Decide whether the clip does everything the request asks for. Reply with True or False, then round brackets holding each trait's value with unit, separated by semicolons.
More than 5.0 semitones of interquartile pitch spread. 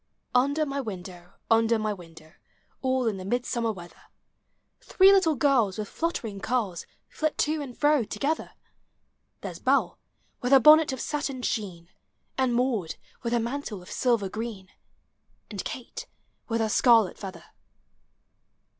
True (5.4 semitones)